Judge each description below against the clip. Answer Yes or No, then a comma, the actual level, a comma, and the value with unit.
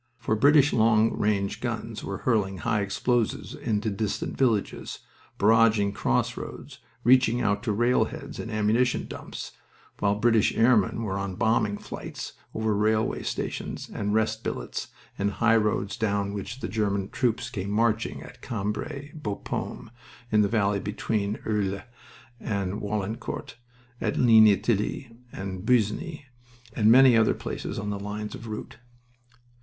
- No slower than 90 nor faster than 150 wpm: Yes, slow, 135 wpm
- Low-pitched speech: Yes, low, 110 Hz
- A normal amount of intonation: No, narrow, 2.2 semitones